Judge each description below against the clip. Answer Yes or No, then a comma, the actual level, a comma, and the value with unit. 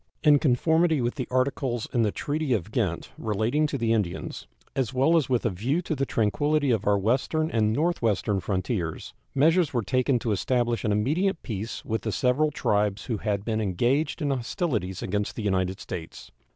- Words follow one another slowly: No, average, 185 wpm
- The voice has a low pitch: Yes, low, 120 Hz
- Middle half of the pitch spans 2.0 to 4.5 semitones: No, wide, 5.4 semitones